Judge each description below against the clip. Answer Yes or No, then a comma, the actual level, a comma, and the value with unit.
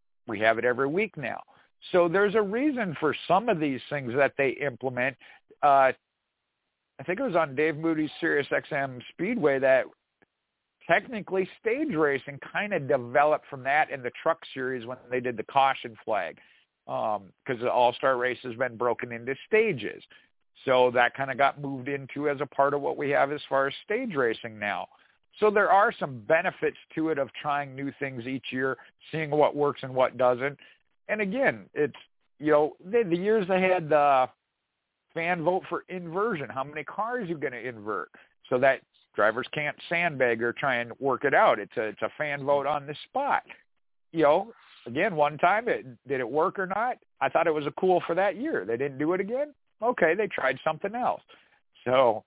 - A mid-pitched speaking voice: Yes, medium, 145 Hz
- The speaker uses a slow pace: No, average, 195 wpm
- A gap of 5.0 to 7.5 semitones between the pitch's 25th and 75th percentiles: Yes, wide, 5.4 semitones